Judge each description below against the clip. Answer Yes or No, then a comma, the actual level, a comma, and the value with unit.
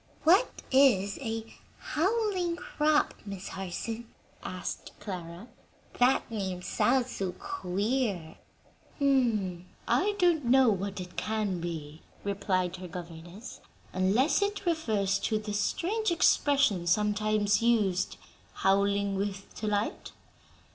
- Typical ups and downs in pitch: No, wide, 6.0 semitones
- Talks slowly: Yes, slow, 105 wpm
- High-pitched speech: Yes, high, 210 Hz